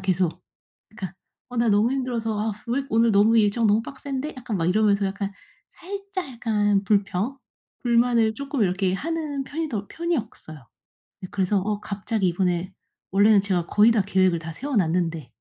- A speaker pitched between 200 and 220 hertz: Yes, high, 215 Hz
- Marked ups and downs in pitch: No, average, 4.2 semitones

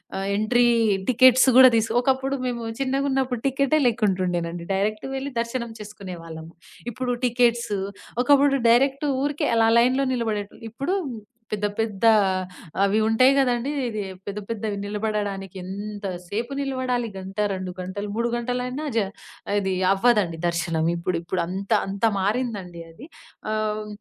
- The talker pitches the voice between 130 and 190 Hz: No, high, 220 Hz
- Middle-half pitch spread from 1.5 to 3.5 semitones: No, average, 4.4 semitones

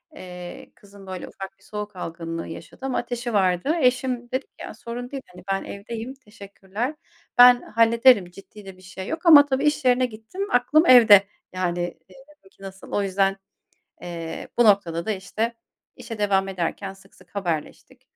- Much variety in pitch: No, average, 4.6 semitones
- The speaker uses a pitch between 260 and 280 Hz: No, high, 205 Hz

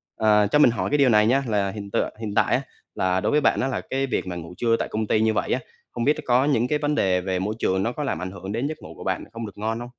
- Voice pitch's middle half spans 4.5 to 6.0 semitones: Yes, average, 4.9 semitones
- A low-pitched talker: Yes, low, 110 Hz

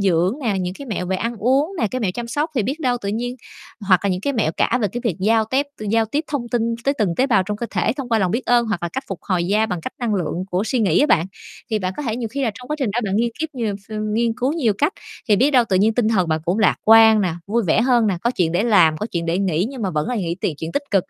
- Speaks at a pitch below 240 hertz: Yes, high, 220 Hz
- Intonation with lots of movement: No, average, 4.6 semitones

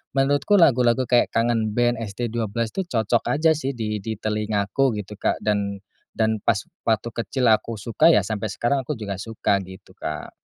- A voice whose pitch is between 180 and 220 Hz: No, low, 115 Hz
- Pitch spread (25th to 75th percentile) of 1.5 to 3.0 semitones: Yes, narrow, 2.6 semitones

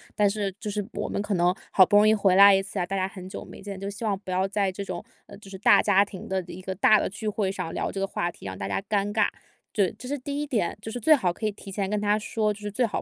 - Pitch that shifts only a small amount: Yes, narrow, 1.9 semitones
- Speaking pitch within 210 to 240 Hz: No, high, 200 Hz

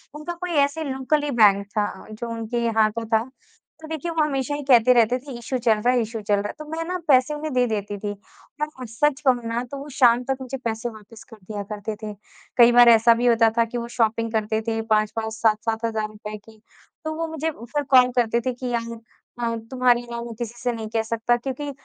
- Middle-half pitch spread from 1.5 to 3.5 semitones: Yes, average, 3.0 semitones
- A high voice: Yes, high, 235 Hz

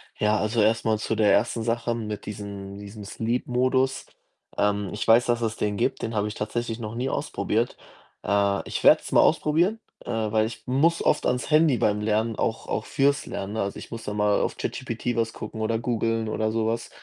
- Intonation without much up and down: Yes, narrow, 2.2 semitones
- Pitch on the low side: Yes, low, 110 Hz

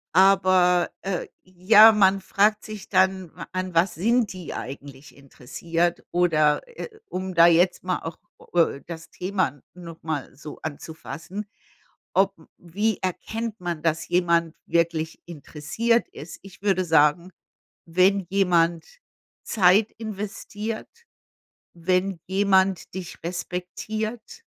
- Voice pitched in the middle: Yes, medium, 180 Hz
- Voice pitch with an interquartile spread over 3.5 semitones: No, average, 2.9 semitones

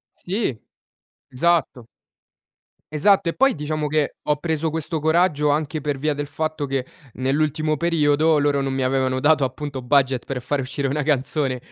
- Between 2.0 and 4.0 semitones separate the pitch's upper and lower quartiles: Yes, narrow, 2.5 semitones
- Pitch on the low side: No, medium, 145 Hz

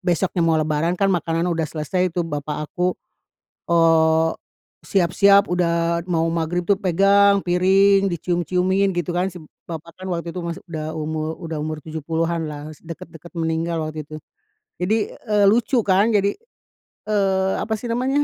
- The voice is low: No, medium, 170 Hz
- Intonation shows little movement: No, average, 3.0 semitones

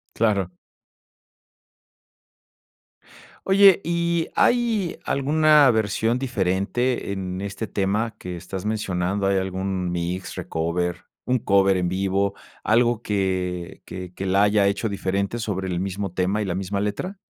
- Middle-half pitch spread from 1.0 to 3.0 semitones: No, average, 3.7 semitones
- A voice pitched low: Yes, low, 100 Hz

